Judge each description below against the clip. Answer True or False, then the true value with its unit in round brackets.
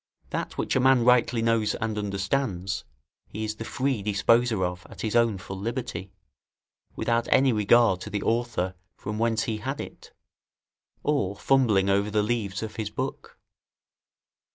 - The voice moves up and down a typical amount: True (3.2 semitones)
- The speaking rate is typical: True (155 wpm)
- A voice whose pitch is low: True (110 Hz)